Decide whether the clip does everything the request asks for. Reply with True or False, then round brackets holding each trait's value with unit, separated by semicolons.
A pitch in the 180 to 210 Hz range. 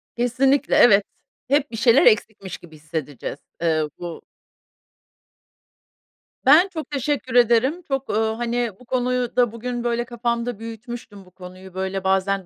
False (235 Hz)